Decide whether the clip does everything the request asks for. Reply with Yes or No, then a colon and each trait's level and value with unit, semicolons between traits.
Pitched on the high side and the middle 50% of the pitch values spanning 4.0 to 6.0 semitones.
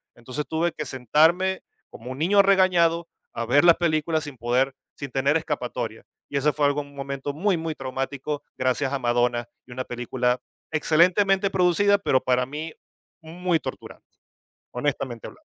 No: medium, 145 Hz; average, 4.6 semitones